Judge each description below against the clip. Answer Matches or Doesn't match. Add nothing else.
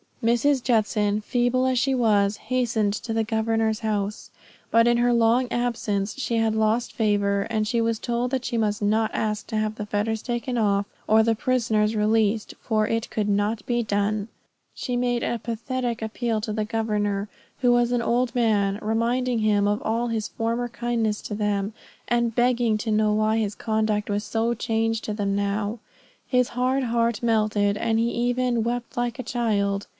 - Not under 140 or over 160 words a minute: Doesn't match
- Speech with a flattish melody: Matches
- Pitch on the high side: Matches